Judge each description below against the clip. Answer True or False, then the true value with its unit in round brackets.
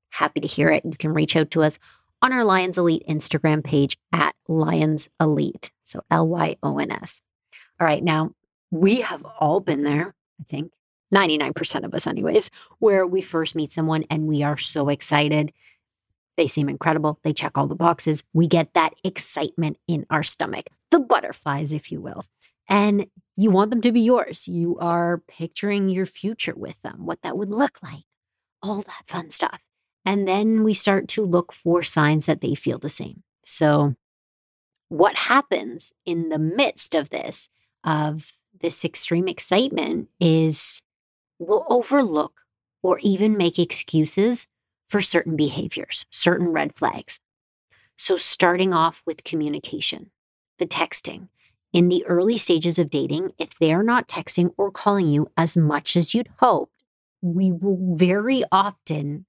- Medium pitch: True (170 Hz)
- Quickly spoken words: False (160 wpm)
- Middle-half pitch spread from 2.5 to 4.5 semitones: True (3.9 semitones)